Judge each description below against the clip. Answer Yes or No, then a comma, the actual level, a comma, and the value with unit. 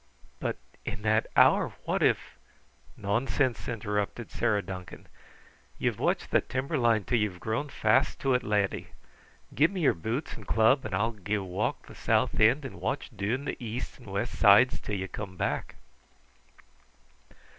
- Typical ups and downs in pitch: Yes, average, 4.0 semitones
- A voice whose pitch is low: Yes, low, 110 Hz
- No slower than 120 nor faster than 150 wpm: No, average, 165 wpm